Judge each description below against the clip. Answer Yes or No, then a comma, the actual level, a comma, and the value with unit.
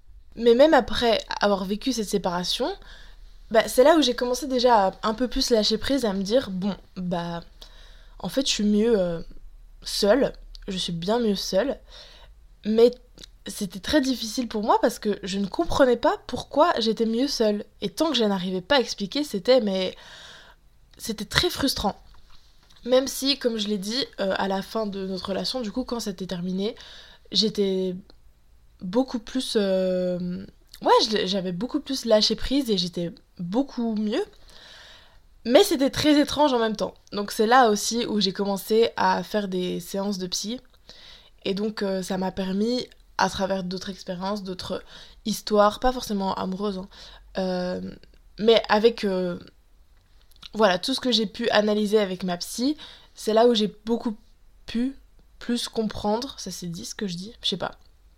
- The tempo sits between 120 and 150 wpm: No, average, 170 wpm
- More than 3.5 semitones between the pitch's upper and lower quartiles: Yes, average, 4.2 semitones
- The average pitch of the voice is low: No, high, 210 Hz